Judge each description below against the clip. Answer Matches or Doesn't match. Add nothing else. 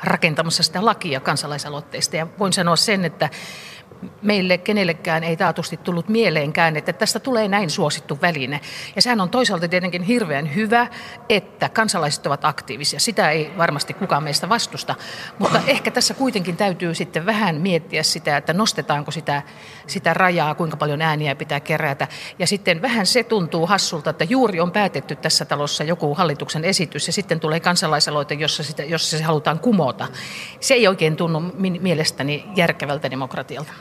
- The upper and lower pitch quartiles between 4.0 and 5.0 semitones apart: Matches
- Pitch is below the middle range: Doesn't match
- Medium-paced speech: Doesn't match